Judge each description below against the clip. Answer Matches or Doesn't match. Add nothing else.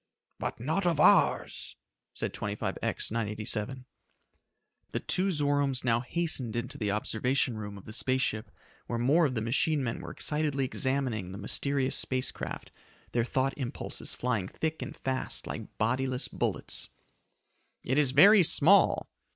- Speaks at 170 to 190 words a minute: Doesn't match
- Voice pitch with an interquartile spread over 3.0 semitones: Matches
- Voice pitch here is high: Doesn't match